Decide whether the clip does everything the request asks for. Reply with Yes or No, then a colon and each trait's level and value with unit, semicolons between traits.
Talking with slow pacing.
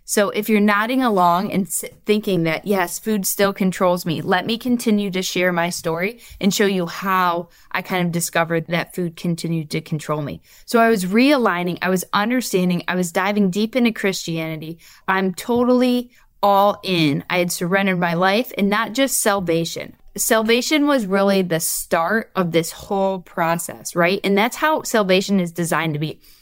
No: average, 175 wpm